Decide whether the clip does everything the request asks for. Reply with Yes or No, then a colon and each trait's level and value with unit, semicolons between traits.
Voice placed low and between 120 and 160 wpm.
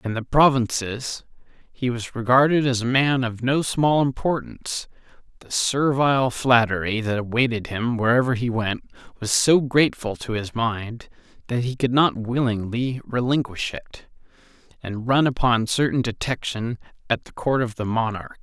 Yes: low, 120 Hz; average, 150 wpm